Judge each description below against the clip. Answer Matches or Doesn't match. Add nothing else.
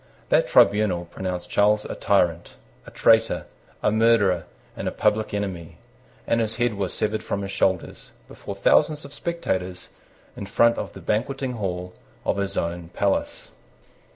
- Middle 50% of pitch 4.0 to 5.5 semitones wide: Doesn't match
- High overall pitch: Doesn't match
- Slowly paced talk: Doesn't match